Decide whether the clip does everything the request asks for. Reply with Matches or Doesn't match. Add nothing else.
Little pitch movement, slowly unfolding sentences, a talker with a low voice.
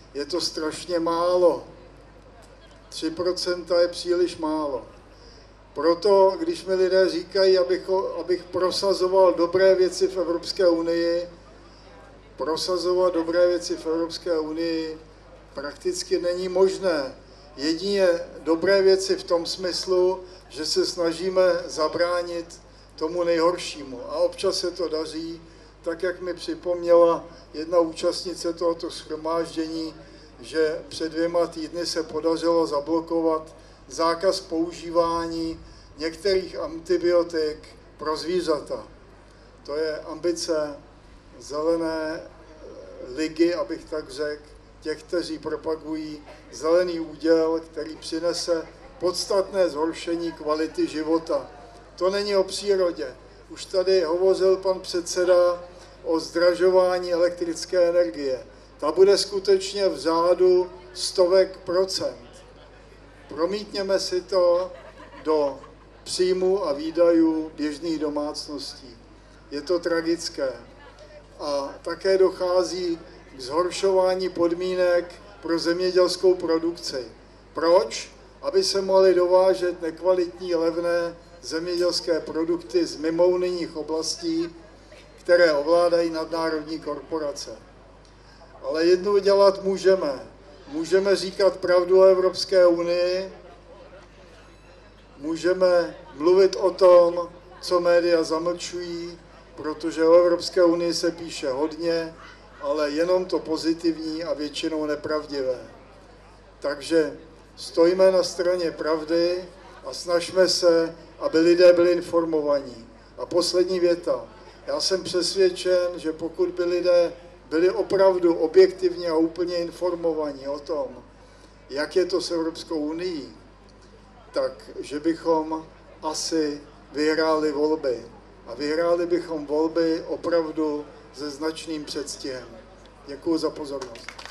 Doesn't match